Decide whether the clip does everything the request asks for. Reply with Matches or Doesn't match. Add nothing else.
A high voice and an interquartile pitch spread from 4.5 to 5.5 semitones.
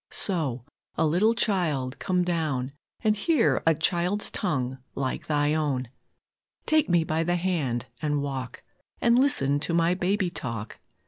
Doesn't match